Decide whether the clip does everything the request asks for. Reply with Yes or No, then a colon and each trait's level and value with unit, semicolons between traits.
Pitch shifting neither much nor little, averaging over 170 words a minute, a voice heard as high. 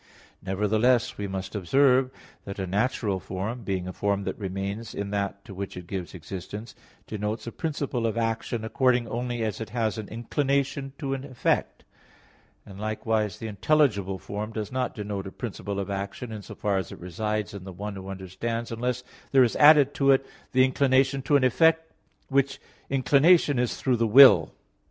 No: average, 4.6 semitones; average, 180 wpm; low, 110 Hz